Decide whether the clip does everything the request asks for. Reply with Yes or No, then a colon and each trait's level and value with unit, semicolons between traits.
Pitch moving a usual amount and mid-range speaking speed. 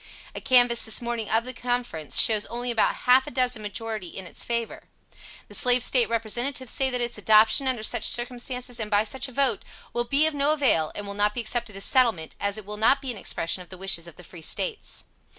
No: average, 3.2 semitones; fast, 230 wpm